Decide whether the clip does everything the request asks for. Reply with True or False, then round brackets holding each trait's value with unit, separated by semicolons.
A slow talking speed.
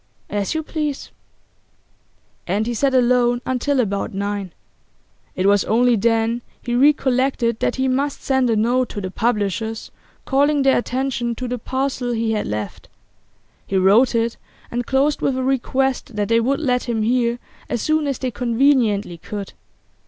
False (160 wpm)